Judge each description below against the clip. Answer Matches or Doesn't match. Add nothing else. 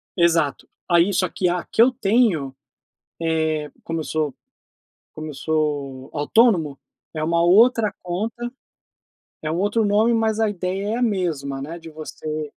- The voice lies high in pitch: Doesn't match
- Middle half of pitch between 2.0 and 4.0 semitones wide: Doesn't match